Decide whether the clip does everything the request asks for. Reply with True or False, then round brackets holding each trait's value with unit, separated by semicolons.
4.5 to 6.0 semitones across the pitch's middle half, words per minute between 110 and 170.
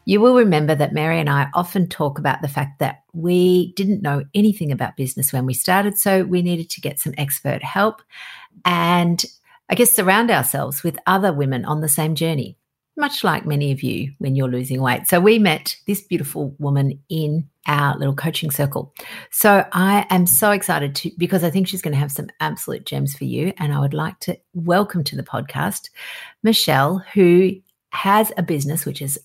False (5.0 semitones; 195 wpm)